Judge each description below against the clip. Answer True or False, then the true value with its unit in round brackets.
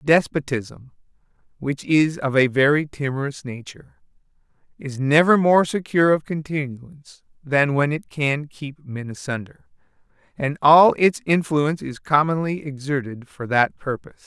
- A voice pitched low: False (145 Hz)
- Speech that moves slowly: True (130 wpm)